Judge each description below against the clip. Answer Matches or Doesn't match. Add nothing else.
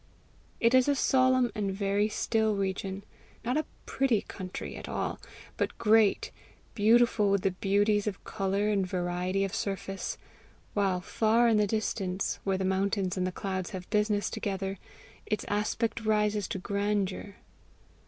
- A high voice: Matches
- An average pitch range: Doesn't match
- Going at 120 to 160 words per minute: Matches